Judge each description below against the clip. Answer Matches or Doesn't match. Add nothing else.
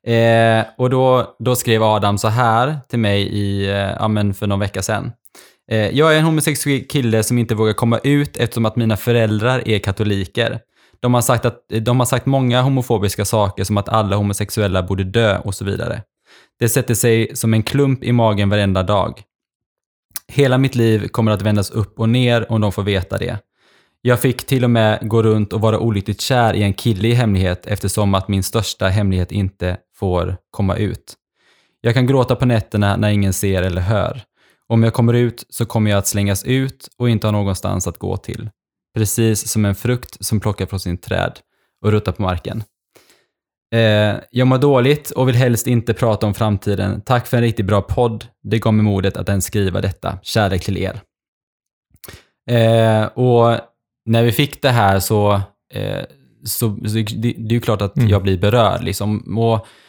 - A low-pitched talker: Matches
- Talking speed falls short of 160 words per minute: Doesn't match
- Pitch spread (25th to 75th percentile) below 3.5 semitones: Matches